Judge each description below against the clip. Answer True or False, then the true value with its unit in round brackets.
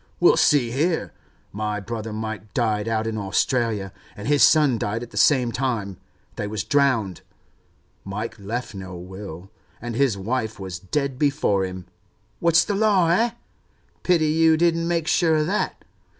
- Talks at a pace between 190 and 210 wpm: False (155 wpm)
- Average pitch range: False (6.8 semitones)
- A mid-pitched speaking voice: False (115 Hz)